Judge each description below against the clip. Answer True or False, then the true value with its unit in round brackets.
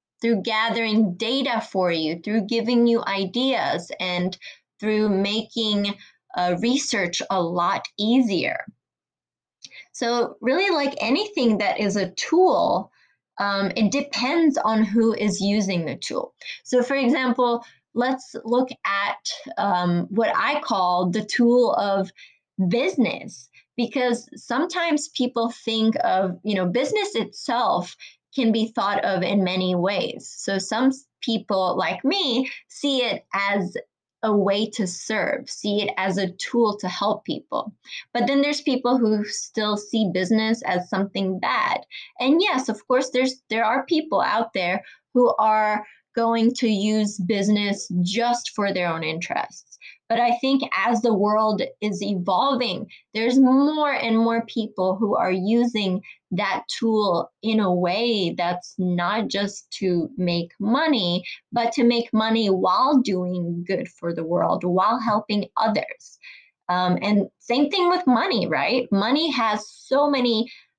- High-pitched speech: True (220 Hz)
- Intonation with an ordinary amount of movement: True (4.3 semitones)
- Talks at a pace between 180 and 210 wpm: False (140 wpm)